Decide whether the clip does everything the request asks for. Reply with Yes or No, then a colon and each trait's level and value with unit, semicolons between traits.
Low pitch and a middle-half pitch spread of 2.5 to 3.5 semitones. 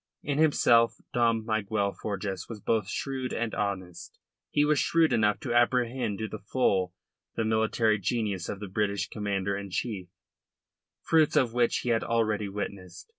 Yes: low, 110 Hz; average, 3.1 semitones